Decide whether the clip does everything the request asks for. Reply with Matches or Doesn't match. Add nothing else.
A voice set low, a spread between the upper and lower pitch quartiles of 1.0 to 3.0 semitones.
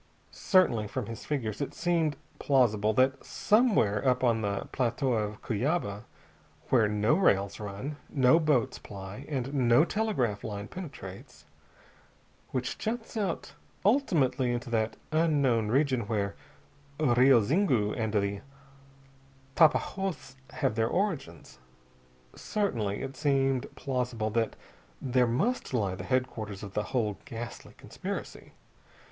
Doesn't match